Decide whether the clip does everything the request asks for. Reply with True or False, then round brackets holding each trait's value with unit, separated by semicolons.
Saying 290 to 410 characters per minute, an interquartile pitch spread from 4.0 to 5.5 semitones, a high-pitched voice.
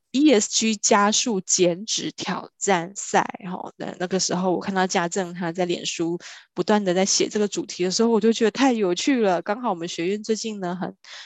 False (295 characters per minute; 3.6 semitones; 195 Hz)